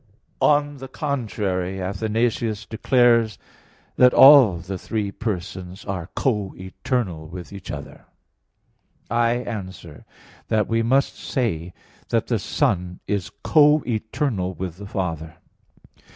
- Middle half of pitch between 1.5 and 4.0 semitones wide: No, average, 4.8 semitones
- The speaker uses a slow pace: Yes, slow, 115 wpm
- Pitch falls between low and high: No, low, 105 Hz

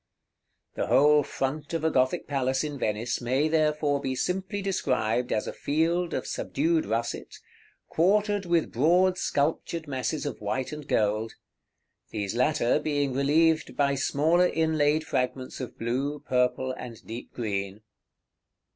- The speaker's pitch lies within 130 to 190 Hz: Yes, medium, 140 Hz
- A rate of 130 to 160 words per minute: Yes, average, 140 wpm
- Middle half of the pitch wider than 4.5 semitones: No, average, 4.1 semitones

